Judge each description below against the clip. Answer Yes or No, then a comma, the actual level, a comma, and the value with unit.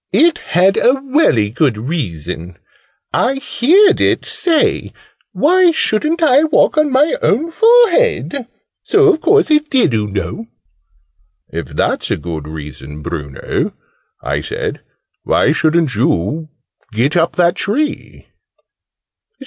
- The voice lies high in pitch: Yes, high, 215 Hz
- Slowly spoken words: Yes, slow, 125 wpm